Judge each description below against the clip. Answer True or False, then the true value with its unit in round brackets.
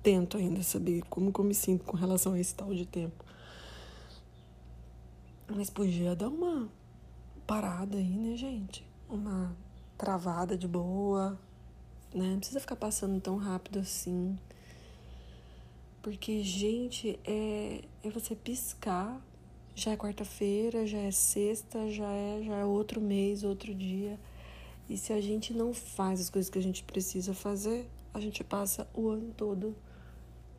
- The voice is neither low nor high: False (195 Hz)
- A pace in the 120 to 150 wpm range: True (145 wpm)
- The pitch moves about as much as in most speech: True (3.1 semitones)